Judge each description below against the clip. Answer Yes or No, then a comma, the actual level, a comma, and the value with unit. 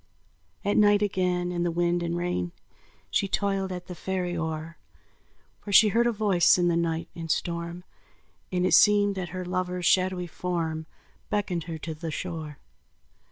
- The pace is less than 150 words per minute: No, average, 165 wpm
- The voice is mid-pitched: Yes, medium, 180 Hz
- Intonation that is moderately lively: No, narrow, 2.1 semitones